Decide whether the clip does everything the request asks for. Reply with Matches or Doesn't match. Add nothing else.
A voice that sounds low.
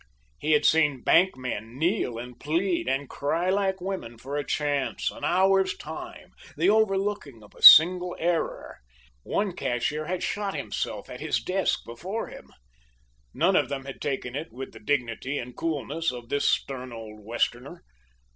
Doesn't match